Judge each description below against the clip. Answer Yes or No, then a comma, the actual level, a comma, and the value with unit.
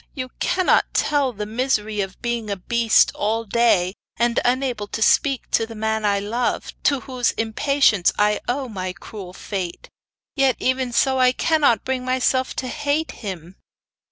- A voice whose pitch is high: Yes, high, 235 Hz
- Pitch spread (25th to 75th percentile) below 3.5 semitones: No, average, 3.8 semitones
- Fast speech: No, average, 165 wpm